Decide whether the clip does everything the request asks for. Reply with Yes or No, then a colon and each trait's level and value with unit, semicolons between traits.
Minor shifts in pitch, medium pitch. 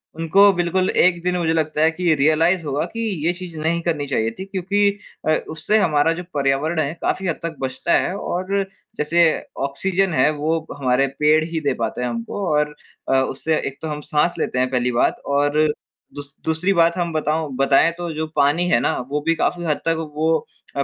No: average, 3.2 semitones; medium, 160 Hz